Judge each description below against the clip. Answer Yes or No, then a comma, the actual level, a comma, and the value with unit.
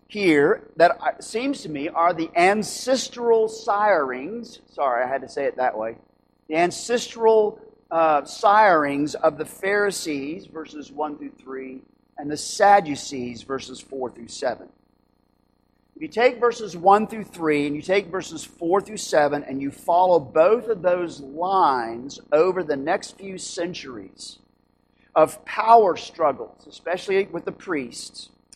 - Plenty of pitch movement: Yes, wide, 6.5 semitones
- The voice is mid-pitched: Yes, medium, 175 Hz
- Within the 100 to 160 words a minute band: Yes, average, 145 wpm